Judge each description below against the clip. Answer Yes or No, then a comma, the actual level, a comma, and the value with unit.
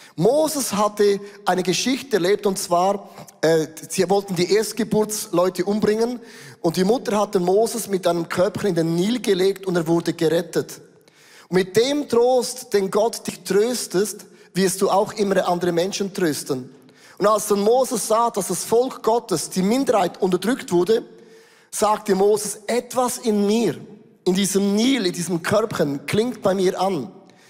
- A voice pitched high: Yes, high, 200 Hz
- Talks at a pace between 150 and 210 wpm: Yes, average, 155 wpm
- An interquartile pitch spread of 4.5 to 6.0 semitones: No, average, 3.4 semitones